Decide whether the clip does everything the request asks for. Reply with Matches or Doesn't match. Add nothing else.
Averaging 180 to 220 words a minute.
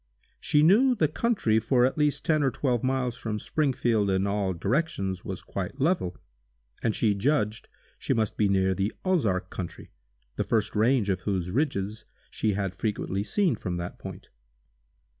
Doesn't match